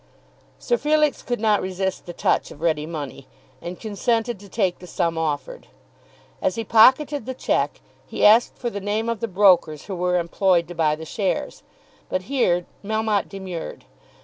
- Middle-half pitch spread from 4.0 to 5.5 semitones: Yes, average, 4.5 semitones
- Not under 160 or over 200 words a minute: Yes, average, 175 wpm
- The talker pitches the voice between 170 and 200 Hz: Yes, high, 190 Hz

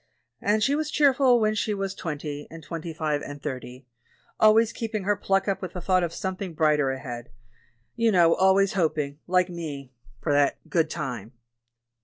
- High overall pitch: No, medium, 175 Hz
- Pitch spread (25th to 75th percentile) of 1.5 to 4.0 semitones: No, wide, 5.4 semitones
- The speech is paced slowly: No, average, 185 wpm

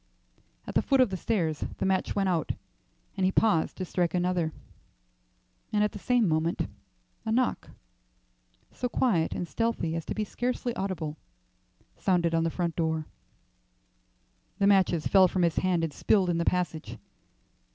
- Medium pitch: Yes, medium, 180 Hz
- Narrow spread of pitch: No, average, 3.7 semitones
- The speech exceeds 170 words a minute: No, average, 160 wpm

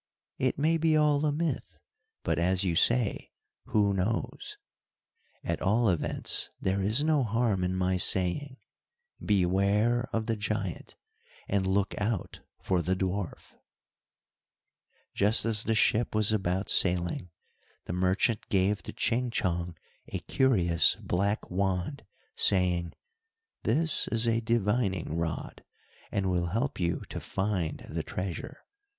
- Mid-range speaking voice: No, low, 100 Hz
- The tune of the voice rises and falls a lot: No, average, 4.1 semitones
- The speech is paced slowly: Yes, slow, 130 wpm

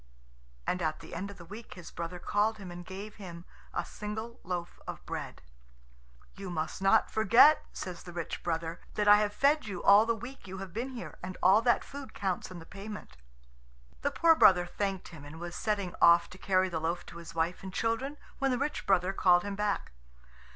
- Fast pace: Yes, fast, 210 wpm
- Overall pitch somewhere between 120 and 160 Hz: No, high, 190 Hz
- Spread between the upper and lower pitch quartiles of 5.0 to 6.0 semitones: No, average, 3.7 semitones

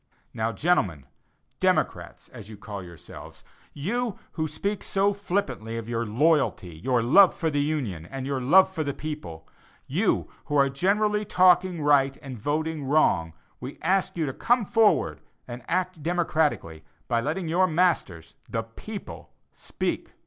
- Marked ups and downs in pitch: Yes, wide, 7.9 semitones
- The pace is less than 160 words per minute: Yes, average, 150 wpm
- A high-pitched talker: No, medium, 150 Hz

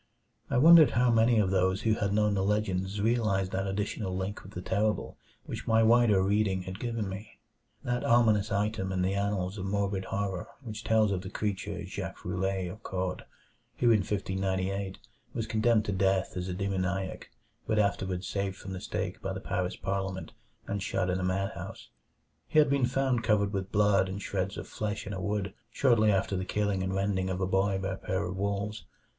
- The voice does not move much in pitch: Yes, narrow, 2.1 semitones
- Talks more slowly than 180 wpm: No, average, 195 wpm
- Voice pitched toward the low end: Yes, low, 100 Hz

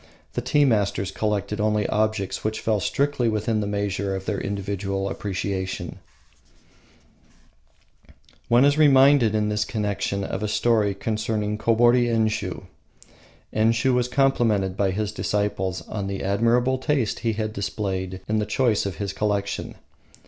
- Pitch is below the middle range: Yes, low, 105 Hz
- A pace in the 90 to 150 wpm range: Yes, average, 140 wpm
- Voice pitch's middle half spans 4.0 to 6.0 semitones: No, narrow, 2.6 semitones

